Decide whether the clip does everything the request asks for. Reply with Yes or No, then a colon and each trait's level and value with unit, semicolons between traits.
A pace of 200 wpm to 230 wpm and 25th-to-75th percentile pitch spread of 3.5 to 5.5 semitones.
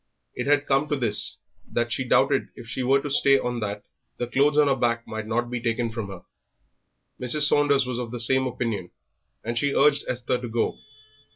No: fast, 205 wpm; average, 3.0 semitones